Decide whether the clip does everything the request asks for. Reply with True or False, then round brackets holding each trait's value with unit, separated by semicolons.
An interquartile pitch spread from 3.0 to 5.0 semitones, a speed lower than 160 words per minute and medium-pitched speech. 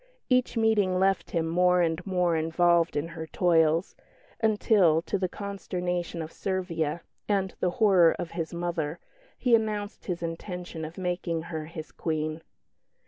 False (2.6 semitones; 145 wpm; 175 Hz)